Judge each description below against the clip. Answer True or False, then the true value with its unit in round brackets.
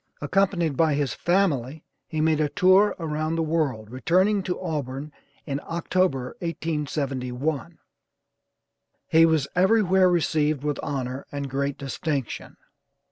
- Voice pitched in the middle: True (155 Hz)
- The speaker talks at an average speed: False (120 wpm)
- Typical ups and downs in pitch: True (3.7 semitones)